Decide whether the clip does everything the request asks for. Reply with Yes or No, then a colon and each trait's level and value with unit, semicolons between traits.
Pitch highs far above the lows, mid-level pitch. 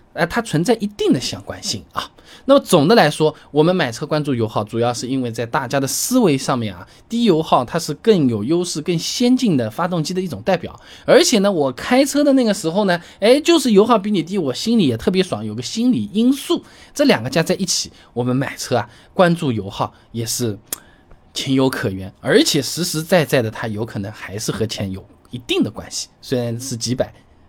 Yes: wide, 8.9 semitones; medium, 155 Hz